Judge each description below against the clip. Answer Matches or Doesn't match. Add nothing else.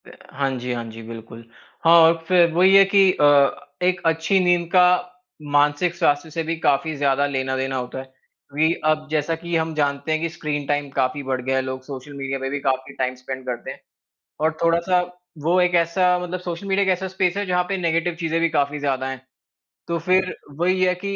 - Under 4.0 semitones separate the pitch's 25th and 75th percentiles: Doesn't match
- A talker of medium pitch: Matches